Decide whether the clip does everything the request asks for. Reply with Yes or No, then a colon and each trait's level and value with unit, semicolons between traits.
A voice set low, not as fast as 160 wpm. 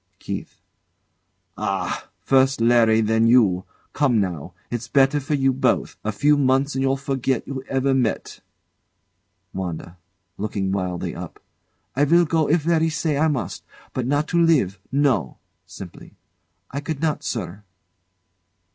Yes: low, 130 Hz; average, 140 wpm